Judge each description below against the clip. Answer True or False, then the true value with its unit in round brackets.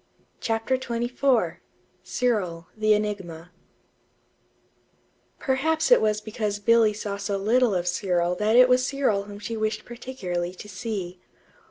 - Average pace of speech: False (130 wpm)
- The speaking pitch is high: True (215 Hz)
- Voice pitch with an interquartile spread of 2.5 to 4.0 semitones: True (3.7 semitones)